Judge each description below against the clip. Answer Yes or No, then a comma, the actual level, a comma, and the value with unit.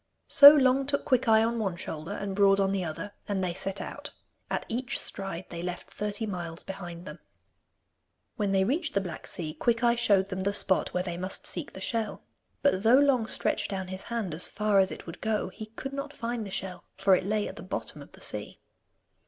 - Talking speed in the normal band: No, fast, 220 wpm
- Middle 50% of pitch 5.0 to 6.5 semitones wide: No, average, 3.7 semitones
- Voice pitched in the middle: No, high, 200 Hz